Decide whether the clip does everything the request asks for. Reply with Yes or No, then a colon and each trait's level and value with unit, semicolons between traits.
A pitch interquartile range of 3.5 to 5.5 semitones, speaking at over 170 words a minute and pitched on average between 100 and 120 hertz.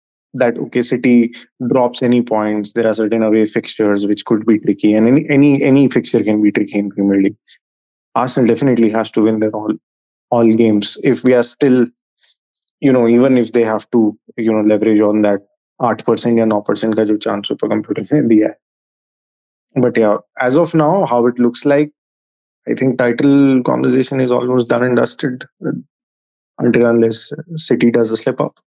No: average, 2.7 semitones; average, 180 wpm; low, 115 Hz